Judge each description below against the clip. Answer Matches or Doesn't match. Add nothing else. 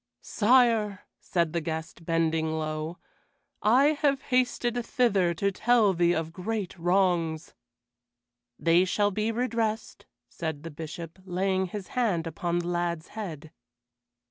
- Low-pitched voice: Doesn't match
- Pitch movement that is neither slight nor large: Matches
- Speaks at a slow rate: Matches